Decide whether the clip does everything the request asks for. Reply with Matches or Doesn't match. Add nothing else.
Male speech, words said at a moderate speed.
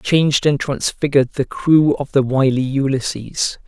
Matches